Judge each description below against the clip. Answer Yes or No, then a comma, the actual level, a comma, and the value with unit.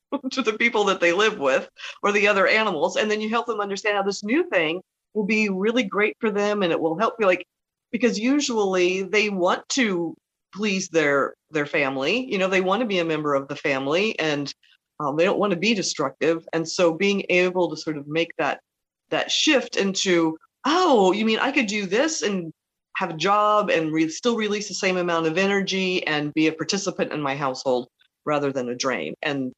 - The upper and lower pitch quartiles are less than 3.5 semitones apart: No, average, 4.9 semitones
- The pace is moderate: No, fast, 215 wpm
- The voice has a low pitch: No, high, 190 Hz